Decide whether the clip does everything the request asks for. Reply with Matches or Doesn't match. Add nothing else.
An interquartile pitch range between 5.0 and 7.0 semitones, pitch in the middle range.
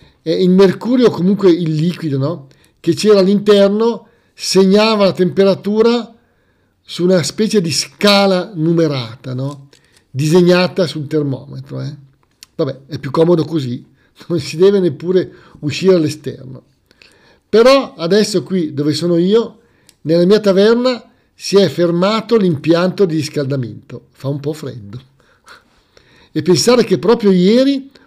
Matches